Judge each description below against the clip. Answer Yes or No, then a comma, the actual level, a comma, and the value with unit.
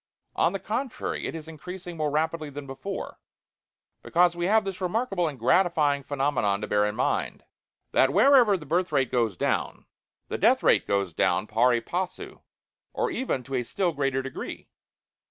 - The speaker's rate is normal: Yes, average, 170 wpm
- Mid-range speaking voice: Yes, medium, 155 Hz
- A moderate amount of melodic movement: No, wide, 5.7 semitones